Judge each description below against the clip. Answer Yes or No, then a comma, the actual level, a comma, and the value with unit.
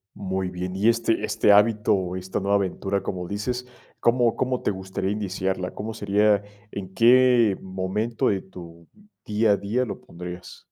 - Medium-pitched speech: No, low, 100 Hz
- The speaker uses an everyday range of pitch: Yes, average, 3.0 semitones